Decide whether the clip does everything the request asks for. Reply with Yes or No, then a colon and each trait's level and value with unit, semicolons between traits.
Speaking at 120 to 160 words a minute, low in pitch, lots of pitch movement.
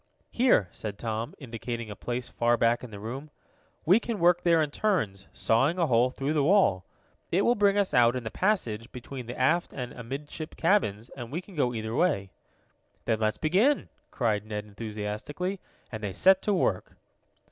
No: average, 185 wpm; low, 125 Hz; wide, 7.8 semitones